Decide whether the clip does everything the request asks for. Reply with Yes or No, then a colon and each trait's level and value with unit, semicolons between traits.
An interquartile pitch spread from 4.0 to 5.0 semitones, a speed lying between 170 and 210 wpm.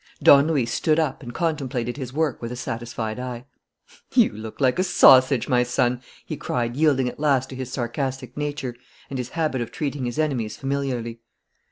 No: average, 2.9 semitones; average, 185 wpm